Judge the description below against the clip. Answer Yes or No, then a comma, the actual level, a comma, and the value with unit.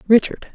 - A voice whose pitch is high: Yes, high, 220 Hz